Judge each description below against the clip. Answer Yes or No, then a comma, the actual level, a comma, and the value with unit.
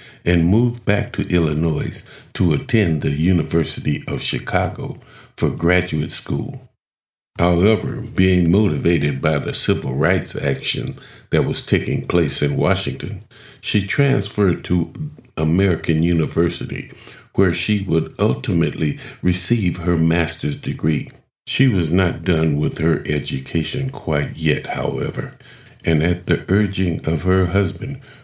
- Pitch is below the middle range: Yes, very low, 90 Hz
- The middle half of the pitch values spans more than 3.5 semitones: Yes, average, 4.2 semitones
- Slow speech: Yes, slow, 125 wpm